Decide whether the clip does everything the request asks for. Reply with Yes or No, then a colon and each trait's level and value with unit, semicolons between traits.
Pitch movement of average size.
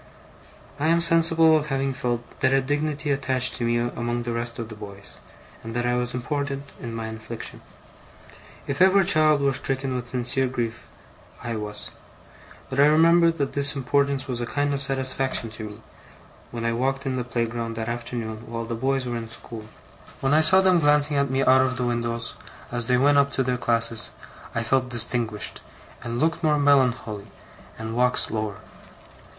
Yes: average, 3.3 semitones